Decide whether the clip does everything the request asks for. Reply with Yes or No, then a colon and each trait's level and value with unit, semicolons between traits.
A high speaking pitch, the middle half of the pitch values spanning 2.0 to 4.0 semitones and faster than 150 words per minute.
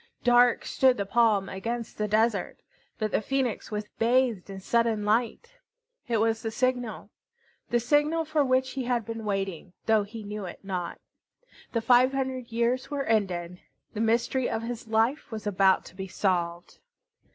Yes: high, 225 Hz; average, 3.3 semitones; average, 165 wpm